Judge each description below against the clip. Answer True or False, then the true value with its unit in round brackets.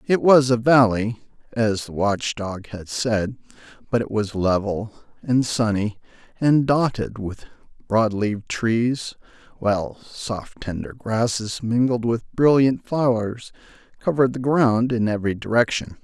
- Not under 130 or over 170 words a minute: True (135 wpm)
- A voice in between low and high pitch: False (115 Hz)